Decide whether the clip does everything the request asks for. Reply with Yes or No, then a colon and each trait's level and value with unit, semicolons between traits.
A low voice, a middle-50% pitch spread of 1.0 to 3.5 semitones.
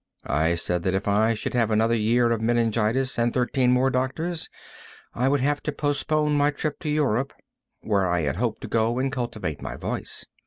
No: low, 120 Hz; average, 3.9 semitones